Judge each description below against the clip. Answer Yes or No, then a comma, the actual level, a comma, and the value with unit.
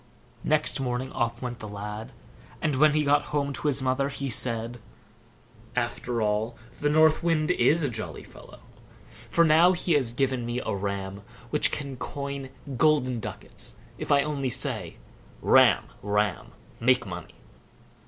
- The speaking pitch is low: Yes, low, 130 Hz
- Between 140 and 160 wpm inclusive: Yes, average, 155 wpm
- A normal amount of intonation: Yes, average, 4.2 semitones